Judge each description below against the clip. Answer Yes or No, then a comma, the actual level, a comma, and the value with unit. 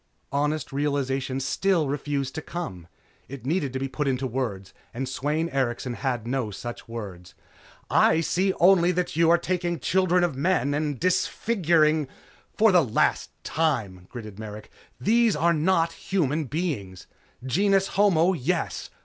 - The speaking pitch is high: No, medium, 150 Hz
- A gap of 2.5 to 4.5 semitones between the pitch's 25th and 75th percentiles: No, average, 5.2 semitones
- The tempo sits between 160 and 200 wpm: No, average, 150 wpm